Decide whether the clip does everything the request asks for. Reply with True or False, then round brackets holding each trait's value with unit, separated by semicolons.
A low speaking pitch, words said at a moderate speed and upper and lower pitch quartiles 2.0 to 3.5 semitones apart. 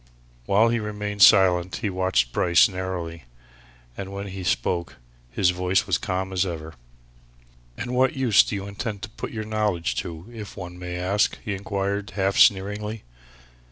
True (95 Hz; 160 wpm; 2.5 semitones)